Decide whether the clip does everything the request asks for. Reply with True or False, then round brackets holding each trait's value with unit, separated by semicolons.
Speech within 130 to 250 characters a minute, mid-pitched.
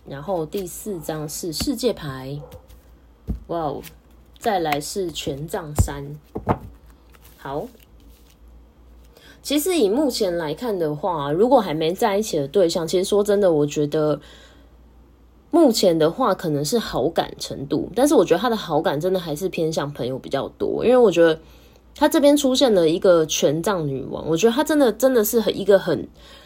True (240 characters per minute; 160 Hz)